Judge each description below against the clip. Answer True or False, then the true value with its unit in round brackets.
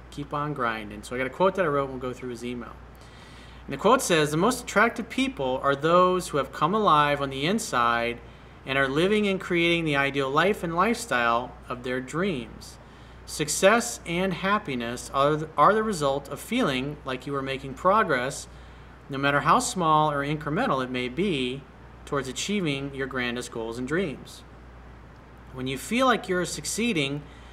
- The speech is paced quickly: False (180 wpm)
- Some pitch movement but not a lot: False (6.3 semitones)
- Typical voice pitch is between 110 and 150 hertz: True (140 Hz)